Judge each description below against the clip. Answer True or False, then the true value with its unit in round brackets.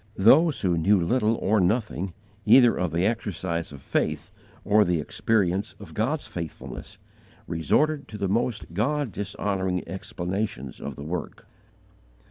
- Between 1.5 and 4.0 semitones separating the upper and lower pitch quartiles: False (4.4 semitones)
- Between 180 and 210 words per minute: False (135 wpm)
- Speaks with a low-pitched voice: True (100 Hz)